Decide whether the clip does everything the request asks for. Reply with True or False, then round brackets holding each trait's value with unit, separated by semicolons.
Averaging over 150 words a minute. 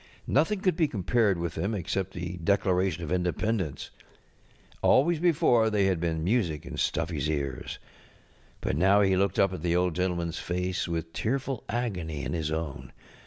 True (165 wpm)